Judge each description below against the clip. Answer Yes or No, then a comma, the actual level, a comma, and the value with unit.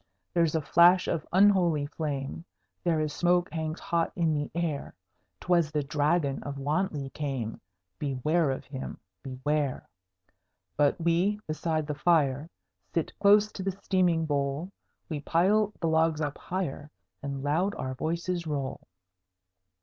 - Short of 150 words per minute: Yes, average, 140 wpm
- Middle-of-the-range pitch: Yes, medium, 155 Hz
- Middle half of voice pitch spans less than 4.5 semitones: Yes, average, 3.3 semitones